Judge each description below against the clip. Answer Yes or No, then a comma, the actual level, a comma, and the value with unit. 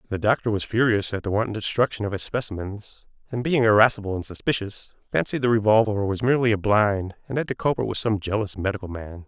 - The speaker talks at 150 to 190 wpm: No, fast, 205 wpm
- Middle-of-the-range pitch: No, low, 105 Hz